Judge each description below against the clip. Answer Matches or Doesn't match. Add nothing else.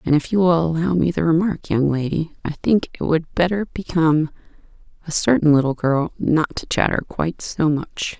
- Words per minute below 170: Doesn't match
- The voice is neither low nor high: Matches